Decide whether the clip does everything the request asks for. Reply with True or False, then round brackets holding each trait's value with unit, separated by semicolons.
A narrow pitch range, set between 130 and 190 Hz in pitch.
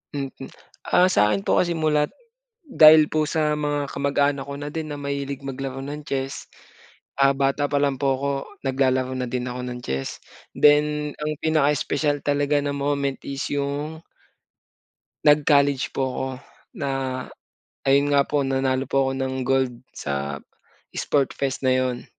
True (1.7 semitones; 140 Hz)